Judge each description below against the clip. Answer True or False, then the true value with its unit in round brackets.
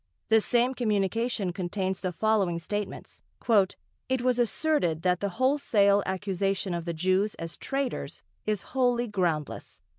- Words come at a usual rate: False (130 wpm)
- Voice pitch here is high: True (200 Hz)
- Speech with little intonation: False (4.7 semitones)